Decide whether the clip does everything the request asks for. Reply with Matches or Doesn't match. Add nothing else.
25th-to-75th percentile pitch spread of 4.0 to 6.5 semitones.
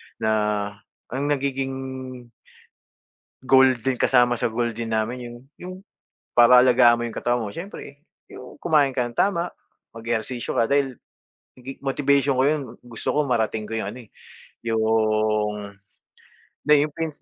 Doesn't match